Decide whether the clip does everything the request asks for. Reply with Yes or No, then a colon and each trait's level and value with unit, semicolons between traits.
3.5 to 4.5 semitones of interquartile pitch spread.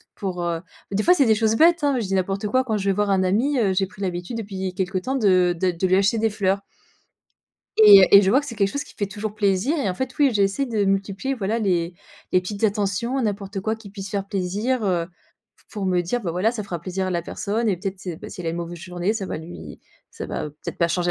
No: average, 3.1 semitones